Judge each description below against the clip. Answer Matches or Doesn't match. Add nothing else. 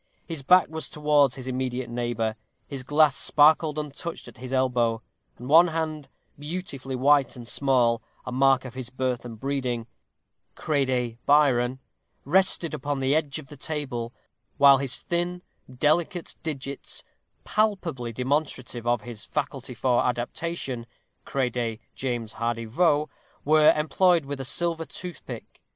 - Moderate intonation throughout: Matches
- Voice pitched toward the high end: Doesn't match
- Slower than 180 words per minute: Matches